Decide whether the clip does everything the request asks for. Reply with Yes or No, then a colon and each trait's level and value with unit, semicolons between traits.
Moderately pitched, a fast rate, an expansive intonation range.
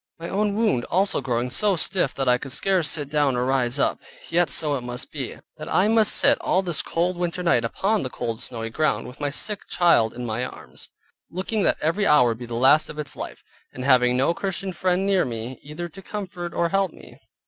Yes: medium, 155 Hz; fast, 225 wpm; wide, 6.8 semitones